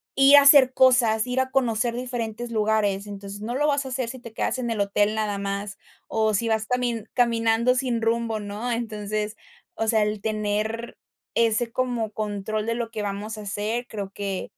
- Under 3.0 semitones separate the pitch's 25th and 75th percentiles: Yes, narrow, 2.4 semitones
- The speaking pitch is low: No, high, 225 Hz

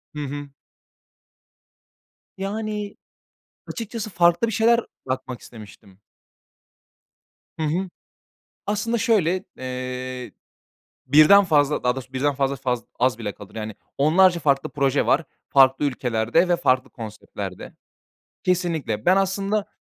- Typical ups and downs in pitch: No, wide, 6.9 semitones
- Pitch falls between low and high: Yes, medium, 145 Hz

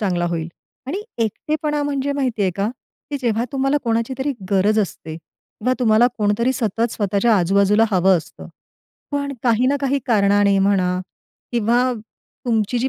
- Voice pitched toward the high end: Yes, high, 225 Hz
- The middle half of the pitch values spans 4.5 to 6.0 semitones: Yes, average, 4.8 semitones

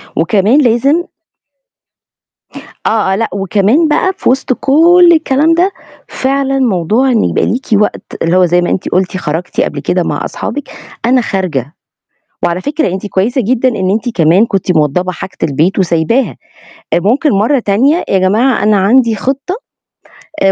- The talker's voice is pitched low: No, high, 220 Hz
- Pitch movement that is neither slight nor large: No, wide, 6.3 semitones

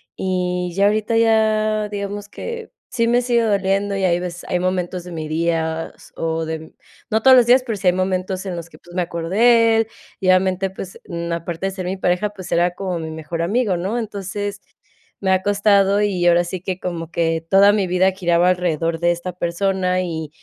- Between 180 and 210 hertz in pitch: Yes, medium, 185 Hz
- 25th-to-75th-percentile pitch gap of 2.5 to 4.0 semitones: Yes, average, 2.9 semitones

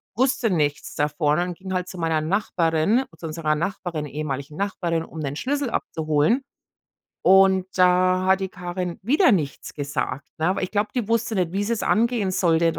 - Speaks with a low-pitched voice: No, medium, 180 Hz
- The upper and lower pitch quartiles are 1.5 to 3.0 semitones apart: No, average, 4.3 semitones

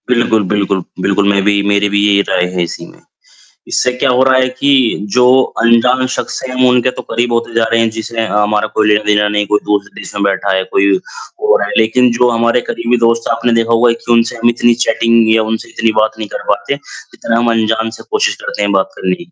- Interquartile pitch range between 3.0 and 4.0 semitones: No, narrow, 2.6 semitones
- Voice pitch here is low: Yes, low, 115 Hz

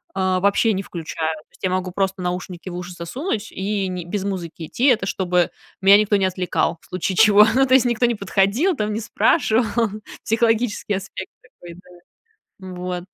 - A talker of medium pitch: No, high, 195 Hz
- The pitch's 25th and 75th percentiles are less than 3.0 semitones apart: No, average, 3.4 semitones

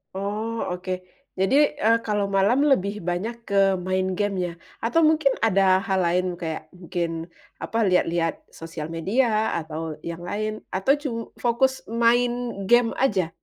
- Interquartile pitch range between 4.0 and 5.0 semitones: Yes, average, 4.7 semitones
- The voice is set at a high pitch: Yes, high, 200 Hz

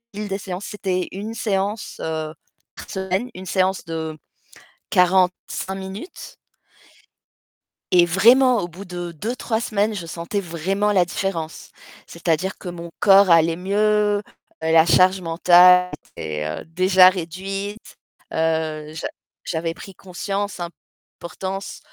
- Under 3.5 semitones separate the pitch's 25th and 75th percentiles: Yes, average, 2.9 semitones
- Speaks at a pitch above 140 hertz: Yes, medium, 185 Hz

